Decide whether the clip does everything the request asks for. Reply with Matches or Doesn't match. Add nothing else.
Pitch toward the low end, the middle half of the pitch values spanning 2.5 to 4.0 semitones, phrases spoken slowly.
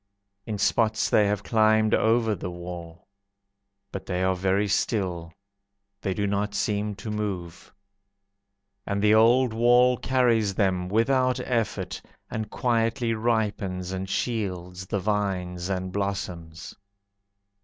Matches